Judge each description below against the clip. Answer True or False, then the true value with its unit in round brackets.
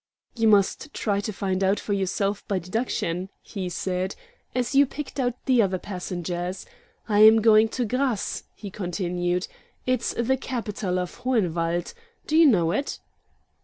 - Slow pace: False (155 wpm)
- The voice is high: True (205 Hz)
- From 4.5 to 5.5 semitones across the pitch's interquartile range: True (4.8 semitones)